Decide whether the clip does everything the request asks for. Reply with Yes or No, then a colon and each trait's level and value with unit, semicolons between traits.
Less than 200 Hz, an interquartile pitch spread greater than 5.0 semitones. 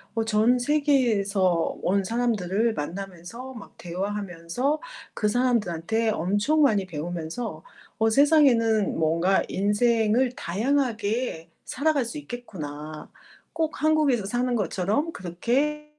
No: high, 220 Hz; wide, 5.4 semitones